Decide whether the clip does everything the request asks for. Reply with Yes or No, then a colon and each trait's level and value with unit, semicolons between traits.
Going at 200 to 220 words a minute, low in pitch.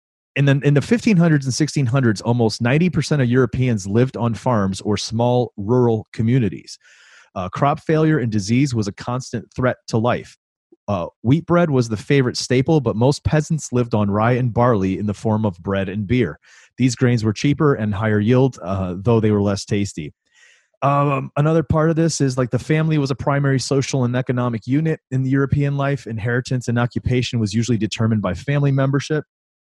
No: average, 190 wpm; low, 125 Hz